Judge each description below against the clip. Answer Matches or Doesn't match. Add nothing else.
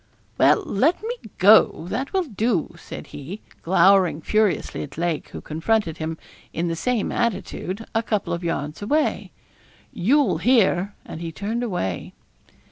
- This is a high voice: Matches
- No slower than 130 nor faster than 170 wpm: Matches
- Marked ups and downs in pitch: Matches